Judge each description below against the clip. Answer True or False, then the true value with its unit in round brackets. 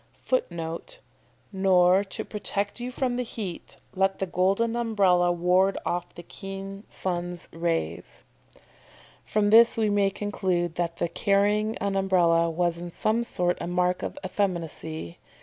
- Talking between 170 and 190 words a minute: False (140 wpm)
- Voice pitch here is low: False (190 Hz)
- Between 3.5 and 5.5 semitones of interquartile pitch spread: False (2.9 semitones)